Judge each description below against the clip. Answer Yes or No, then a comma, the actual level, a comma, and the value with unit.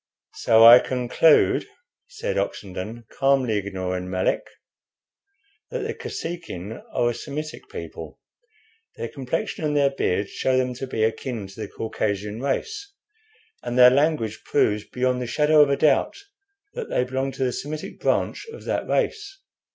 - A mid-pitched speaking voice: No, low, 125 Hz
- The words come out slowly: No, average, 150 wpm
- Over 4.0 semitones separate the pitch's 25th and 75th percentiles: Yes, average, 5.2 semitones